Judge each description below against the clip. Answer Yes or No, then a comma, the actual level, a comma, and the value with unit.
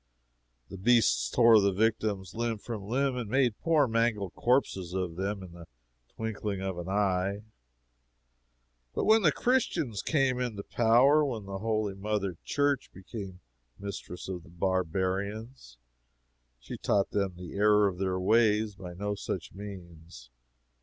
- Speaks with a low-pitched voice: Yes, low, 100 Hz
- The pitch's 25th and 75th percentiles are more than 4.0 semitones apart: No, average, 3.6 semitones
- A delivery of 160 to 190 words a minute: No, average, 145 wpm